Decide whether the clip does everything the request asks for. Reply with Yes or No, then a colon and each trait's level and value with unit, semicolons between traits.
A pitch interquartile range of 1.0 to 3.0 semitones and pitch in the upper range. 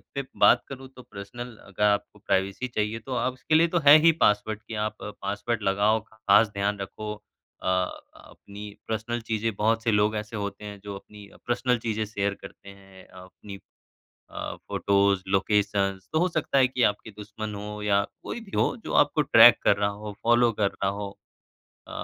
No: narrow, 2.4 semitones; low, 105 Hz